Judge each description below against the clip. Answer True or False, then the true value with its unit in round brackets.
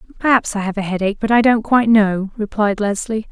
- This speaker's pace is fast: True (215 wpm)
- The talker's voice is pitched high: True (210 Hz)